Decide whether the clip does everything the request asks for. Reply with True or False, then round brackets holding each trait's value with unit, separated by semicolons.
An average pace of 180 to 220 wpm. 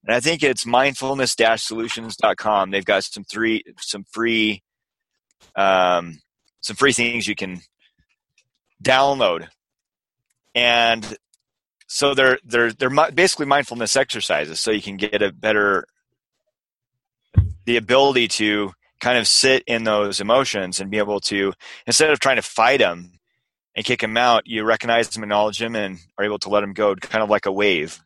False (155 wpm)